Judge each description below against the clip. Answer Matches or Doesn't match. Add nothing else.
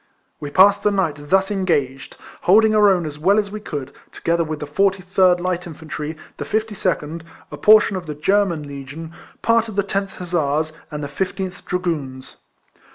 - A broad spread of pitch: Doesn't match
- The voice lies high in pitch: Doesn't match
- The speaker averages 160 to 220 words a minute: Matches